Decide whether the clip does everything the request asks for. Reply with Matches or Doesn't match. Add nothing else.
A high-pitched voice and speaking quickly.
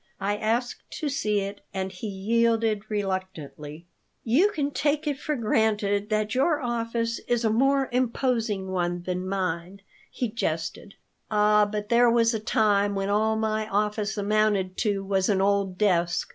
Doesn't match